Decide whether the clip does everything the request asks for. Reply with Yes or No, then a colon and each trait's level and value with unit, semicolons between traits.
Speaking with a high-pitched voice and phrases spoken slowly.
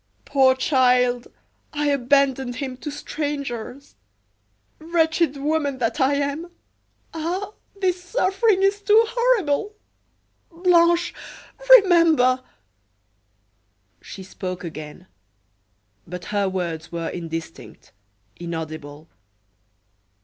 Yes: very high, 275 Hz; slow, 90 wpm